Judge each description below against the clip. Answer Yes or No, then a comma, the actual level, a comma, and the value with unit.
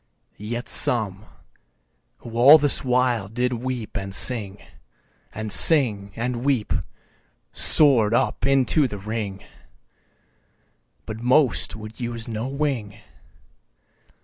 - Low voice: Yes, low, 115 Hz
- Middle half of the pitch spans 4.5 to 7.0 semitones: No, average, 3.3 semitones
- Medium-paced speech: No, slow, 110 wpm